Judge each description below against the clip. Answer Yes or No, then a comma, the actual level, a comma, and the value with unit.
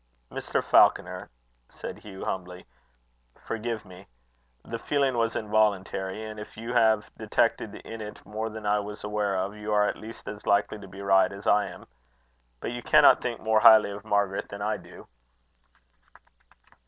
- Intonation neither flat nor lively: No, narrow, 1.6 semitones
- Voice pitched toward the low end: Yes, low, 105 Hz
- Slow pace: No, average, 165 wpm